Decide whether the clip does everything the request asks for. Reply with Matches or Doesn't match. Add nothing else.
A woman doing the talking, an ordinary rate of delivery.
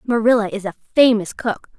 Matches